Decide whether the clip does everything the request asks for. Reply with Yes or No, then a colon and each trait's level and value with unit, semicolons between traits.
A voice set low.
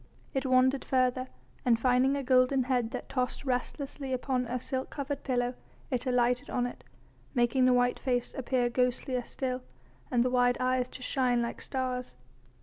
No: very high, 255 Hz